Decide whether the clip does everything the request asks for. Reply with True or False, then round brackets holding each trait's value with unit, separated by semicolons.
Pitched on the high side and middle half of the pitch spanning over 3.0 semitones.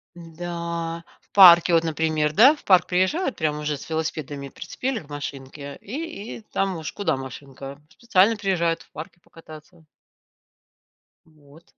False (165 Hz; 3.6 semitones)